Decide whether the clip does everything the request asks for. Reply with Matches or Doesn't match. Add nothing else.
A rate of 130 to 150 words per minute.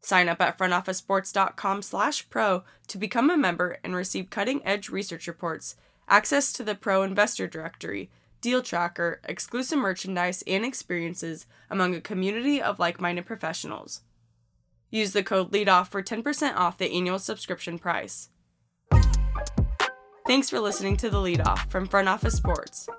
Matches